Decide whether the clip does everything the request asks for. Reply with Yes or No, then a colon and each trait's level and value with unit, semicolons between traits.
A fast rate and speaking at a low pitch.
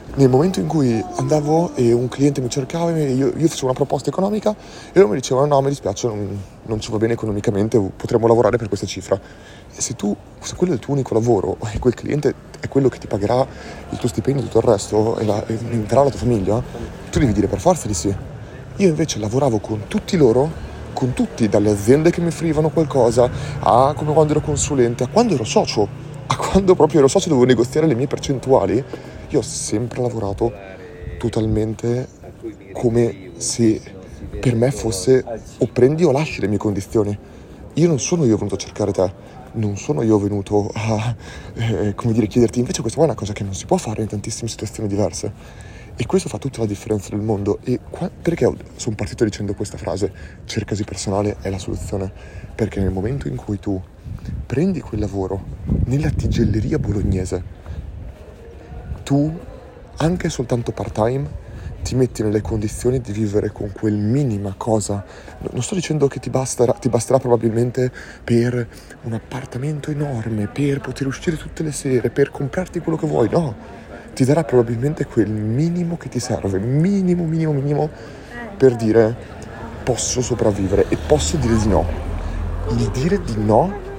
Yes: fast, 180 wpm; low, 115 Hz